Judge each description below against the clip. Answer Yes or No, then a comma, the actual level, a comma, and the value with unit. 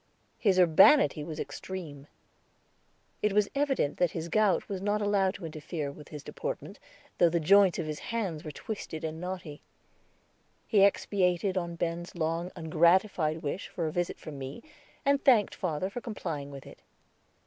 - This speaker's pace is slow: No, average, 160 wpm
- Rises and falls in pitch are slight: No, average, 4.3 semitones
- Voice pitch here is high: No, medium, 175 Hz